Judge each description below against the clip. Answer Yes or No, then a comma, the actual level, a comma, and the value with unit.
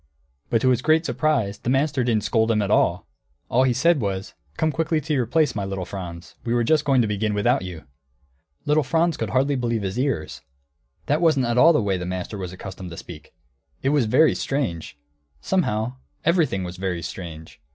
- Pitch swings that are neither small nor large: No, wide, 7.1 semitones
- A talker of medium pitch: No, low, 120 Hz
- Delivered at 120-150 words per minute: No, average, 200 wpm